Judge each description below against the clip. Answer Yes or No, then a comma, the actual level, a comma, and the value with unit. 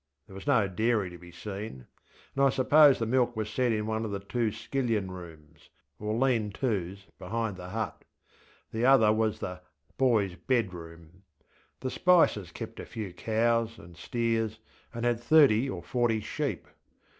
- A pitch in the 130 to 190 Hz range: No, low, 110 Hz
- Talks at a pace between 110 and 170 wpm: Yes, average, 160 wpm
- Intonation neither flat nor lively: Yes, average, 3.8 semitones